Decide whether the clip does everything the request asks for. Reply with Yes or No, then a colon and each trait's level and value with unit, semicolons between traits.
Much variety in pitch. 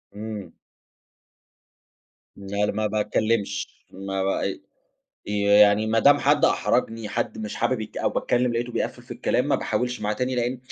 No: average, 2.9 semitones